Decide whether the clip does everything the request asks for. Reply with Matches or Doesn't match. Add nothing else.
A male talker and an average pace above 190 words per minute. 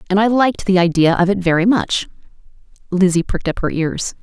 Doesn't match